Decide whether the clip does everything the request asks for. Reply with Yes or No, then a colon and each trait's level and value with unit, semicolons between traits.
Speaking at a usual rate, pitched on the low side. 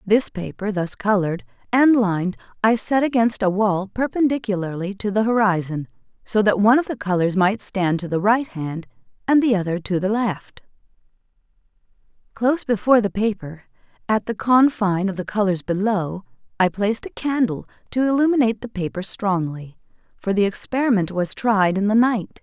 No: average, 165 wpm; high, 205 Hz